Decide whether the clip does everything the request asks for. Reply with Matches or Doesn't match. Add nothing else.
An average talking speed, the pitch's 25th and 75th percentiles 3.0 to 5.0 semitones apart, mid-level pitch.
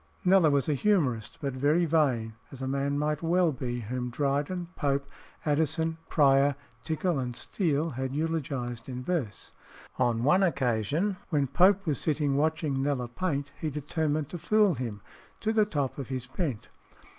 Matches